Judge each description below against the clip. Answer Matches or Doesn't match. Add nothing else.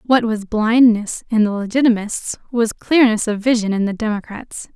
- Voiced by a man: Doesn't match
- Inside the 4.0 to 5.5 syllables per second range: Matches